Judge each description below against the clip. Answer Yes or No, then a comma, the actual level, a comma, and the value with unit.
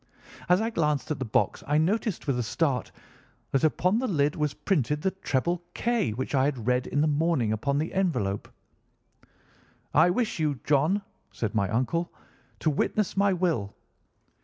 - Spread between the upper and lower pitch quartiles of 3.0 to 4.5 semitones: No, wide, 5.5 semitones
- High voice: No, medium, 150 Hz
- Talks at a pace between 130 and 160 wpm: No, average, 170 wpm